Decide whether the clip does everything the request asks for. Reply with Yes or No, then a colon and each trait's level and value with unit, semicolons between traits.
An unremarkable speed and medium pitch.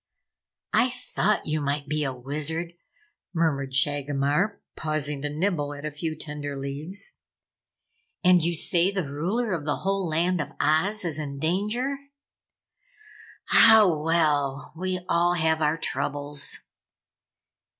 No: slow, 130 wpm; medium, 155 Hz